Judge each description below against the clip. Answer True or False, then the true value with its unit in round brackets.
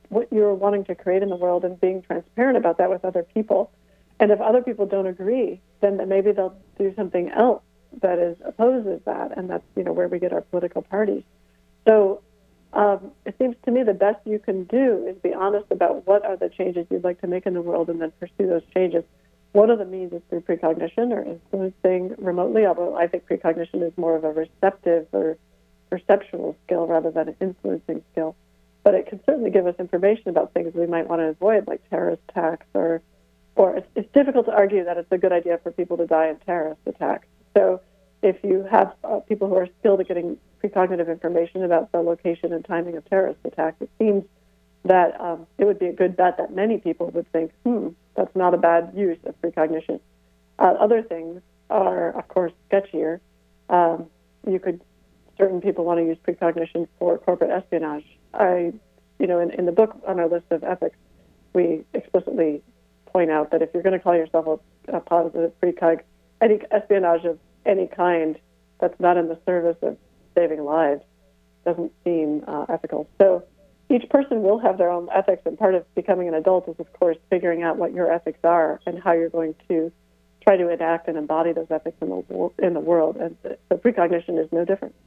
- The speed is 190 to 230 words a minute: True (205 wpm)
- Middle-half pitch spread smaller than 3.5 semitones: True (2.9 semitones)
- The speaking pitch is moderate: True (175 Hz)